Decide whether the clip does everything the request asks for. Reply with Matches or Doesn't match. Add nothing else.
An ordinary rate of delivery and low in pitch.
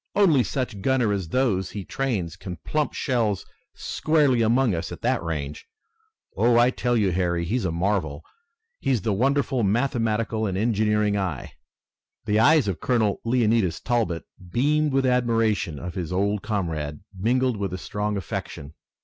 Matches